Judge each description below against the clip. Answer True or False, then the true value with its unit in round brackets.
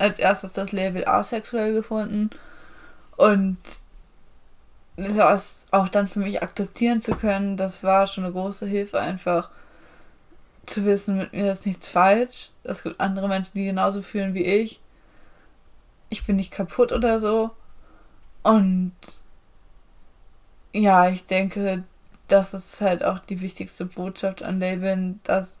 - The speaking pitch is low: False (195 Hz)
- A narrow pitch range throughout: True (1.7 semitones)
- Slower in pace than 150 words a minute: True (135 wpm)